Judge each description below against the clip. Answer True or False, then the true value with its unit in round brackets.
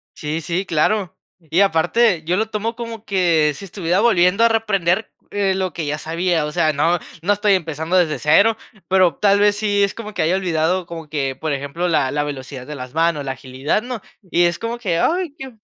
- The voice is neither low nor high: True (175 Hz)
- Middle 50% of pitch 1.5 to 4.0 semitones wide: False (4.7 semitones)